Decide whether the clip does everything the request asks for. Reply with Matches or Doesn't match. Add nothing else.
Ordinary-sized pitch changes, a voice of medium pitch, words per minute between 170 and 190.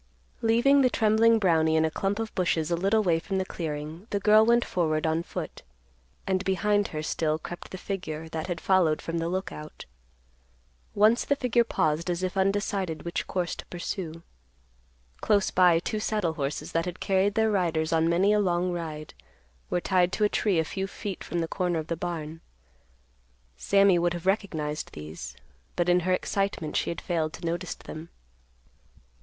Matches